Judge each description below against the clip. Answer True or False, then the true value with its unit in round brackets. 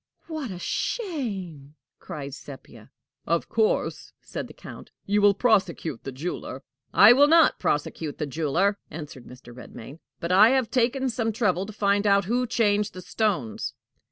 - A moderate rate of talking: True (155 wpm)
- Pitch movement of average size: False (7.2 semitones)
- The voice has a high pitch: True (200 Hz)